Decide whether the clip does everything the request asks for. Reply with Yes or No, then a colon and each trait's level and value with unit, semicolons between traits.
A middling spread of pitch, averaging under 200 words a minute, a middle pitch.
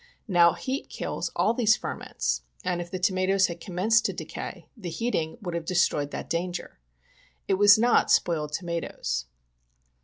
Yes: average, 3.3 semitones; average, 155 wpm; medium, 180 Hz